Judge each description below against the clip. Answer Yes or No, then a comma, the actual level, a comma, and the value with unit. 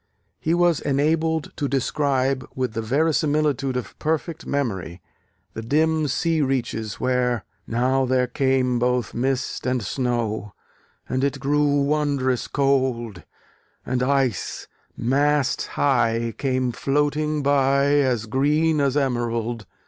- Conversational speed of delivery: No, slow, 120 wpm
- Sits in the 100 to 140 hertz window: Yes, low, 135 Hz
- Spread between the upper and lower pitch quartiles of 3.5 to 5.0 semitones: No, average, 2.9 semitones